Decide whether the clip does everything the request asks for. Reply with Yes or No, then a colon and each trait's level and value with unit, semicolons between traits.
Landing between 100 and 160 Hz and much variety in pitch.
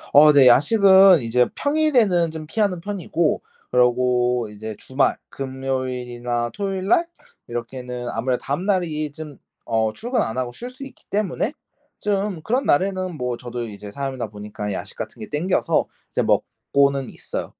Yes: medium, 140 Hz; wide, 7.5 semitones